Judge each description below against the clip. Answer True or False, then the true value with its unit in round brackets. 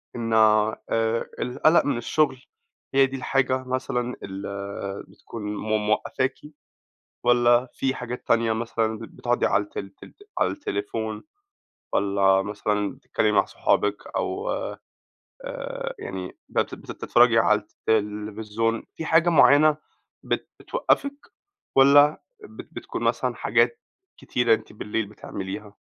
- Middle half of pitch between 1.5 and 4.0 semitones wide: True (3.7 semitones)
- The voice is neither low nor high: False (115 Hz)